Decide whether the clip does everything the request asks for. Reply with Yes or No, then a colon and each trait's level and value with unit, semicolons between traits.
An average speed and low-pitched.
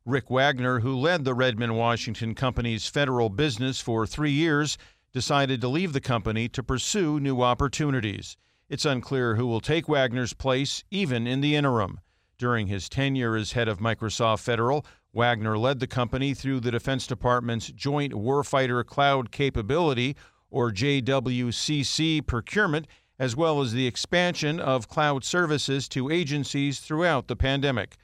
Yes: average, 150 wpm; low, 130 Hz